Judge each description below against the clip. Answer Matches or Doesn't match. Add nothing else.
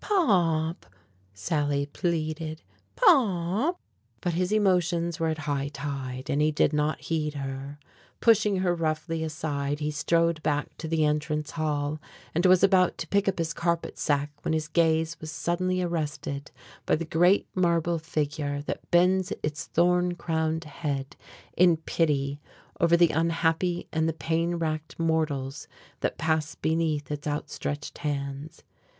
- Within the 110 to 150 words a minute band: Matches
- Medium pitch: Matches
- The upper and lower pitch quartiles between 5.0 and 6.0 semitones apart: Doesn't match